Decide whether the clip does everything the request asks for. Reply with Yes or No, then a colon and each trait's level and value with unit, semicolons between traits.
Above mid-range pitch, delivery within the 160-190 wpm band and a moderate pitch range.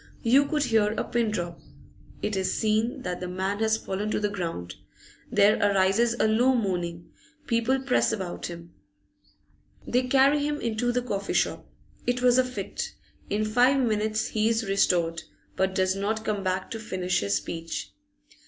Yes: high, 215 Hz; average, 170 wpm; average, 4.2 semitones